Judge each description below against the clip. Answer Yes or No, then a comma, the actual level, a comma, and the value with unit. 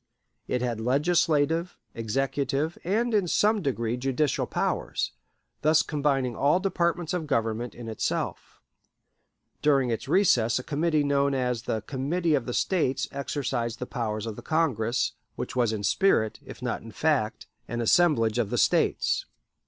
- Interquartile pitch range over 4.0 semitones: Yes, average, 5.2 semitones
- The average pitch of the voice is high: No, low, 135 Hz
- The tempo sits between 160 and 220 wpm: No, average, 150 wpm